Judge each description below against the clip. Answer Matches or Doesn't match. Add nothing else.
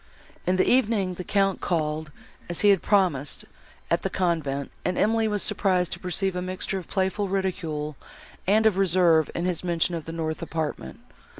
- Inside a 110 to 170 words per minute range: Doesn't match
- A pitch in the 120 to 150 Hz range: Doesn't match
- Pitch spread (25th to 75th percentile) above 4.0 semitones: Doesn't match